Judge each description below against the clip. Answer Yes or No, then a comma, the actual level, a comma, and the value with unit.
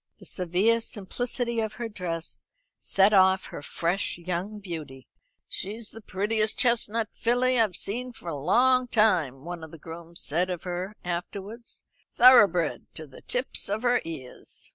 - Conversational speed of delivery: Yes, average, 155 wpm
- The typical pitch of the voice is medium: No, high, 195 Hz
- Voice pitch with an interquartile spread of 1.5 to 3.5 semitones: No, average, 5.0 semitones